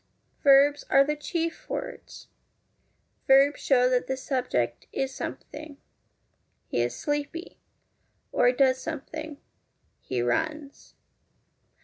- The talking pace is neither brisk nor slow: No, slow, 100 wpm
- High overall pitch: Yes, very high, 275 Hz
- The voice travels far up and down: No, average, 2.7 semitones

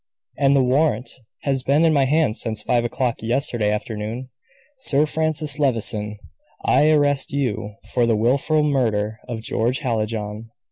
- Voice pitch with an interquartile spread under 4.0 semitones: No, average, 4.3 semitones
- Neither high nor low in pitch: No, low, 125 Hz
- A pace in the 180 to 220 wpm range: No, average, 145 wpm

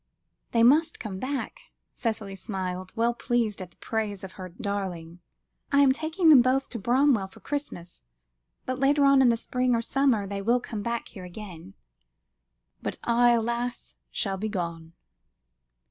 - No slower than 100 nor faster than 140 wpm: No, average, 160 wpm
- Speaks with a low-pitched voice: No, high, 230 Hz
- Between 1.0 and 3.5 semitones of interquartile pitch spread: No, average, 5.0 semitones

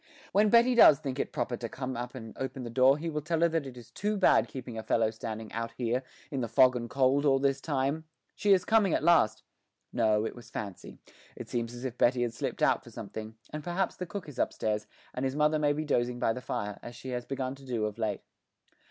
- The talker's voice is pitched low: Yes, low, 130 Hz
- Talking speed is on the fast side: Yes, fast, 245 wpm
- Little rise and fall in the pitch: No, average, 4.5 semitones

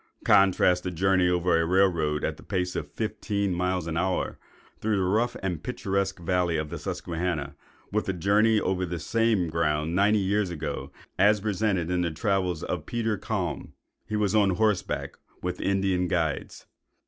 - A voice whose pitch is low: Yes, very low, 95 Hz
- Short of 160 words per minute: No, average, 175 wpm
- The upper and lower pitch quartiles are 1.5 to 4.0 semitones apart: Yes, narrow, 2.6 semitones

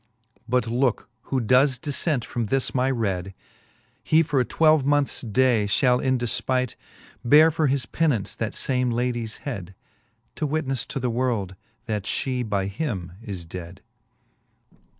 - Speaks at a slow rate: No, average, 150 wpm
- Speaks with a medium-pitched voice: No, low, 125 Hz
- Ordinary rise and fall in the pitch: Yes, average, 4.0 semitones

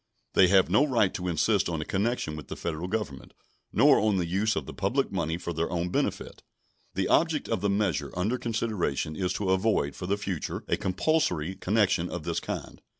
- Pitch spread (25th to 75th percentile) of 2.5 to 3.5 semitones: No, average, 3.9 semitones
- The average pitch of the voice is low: Yes, very low, 95 Hz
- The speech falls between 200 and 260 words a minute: Yes, fast, 205 wpm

